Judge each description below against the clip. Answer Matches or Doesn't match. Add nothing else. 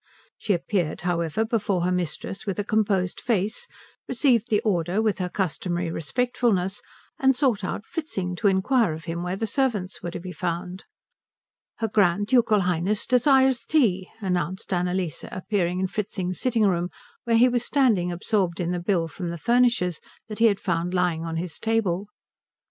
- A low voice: Doesn't match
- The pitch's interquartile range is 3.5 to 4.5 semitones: Matches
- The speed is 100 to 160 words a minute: Doesn't match